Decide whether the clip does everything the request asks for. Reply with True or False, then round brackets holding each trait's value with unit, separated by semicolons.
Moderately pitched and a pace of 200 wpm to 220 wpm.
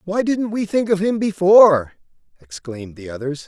False (170 Hz; 175 wpm)